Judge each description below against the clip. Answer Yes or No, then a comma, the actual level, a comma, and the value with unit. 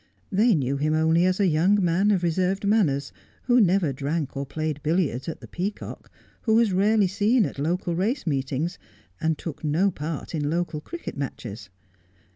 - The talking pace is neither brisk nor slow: Yes, average, 185 wpm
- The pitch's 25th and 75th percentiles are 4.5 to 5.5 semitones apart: Yes, average, 4.9 semitones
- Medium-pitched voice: Yes, medium, 170 Hz